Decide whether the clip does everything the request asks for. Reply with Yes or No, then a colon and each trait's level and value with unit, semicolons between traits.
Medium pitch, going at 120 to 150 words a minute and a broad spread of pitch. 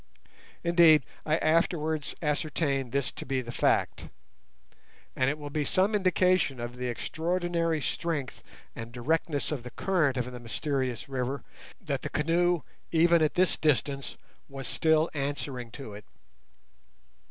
No: medium, 145 Hz; average, 140 wpm; average, 4.3 semitones